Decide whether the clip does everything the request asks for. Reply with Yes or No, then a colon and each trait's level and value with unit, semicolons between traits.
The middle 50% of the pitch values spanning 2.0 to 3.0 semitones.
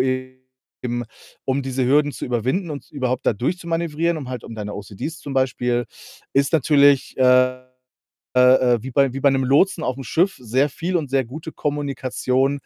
Yes: narrow, 2.6 semitones